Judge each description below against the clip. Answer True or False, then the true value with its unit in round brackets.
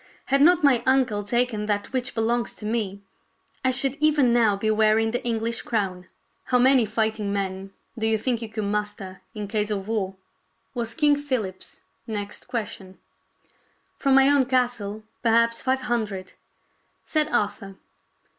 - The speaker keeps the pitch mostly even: False (3.4 semitones)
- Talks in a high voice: True (225 Hz)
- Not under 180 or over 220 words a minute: False (155 wpm)